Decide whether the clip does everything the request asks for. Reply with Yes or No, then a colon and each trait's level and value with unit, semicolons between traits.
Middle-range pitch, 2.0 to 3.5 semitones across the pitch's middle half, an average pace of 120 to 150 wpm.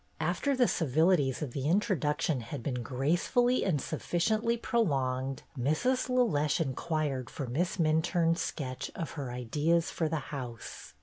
No: medium, 155 Hz; average, 5.0 semitones; slow, 135 wpm